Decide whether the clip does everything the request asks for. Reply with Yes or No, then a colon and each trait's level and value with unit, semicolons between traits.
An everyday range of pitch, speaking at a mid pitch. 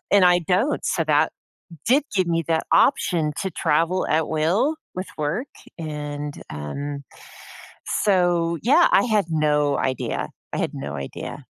Yes: average, 4.3 semitones; medium, 165 Hz